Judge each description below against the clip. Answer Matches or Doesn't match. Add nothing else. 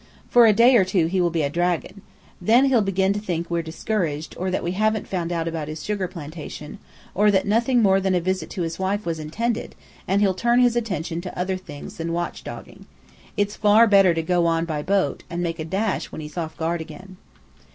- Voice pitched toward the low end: Doesn't match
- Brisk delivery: Matches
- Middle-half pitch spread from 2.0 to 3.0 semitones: Doesn't match